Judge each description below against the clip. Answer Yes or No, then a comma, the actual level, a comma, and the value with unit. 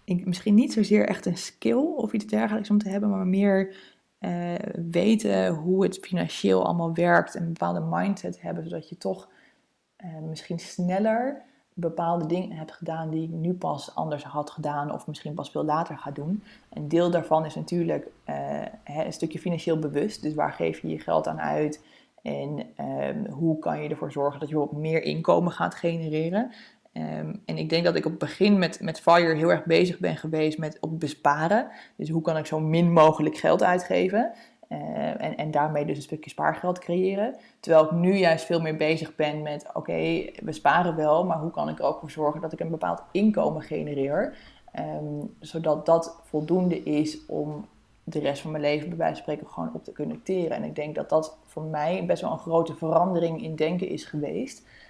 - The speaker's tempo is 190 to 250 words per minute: Yes, fast, 200 wpm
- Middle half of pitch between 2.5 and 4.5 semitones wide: Yes, average, 3.0 semitones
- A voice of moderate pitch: Yes, medium, 160 Hz